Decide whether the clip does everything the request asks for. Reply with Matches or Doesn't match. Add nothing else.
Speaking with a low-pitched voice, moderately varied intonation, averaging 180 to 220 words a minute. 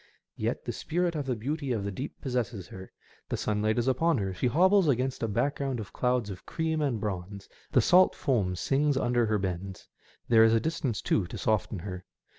Doesn't match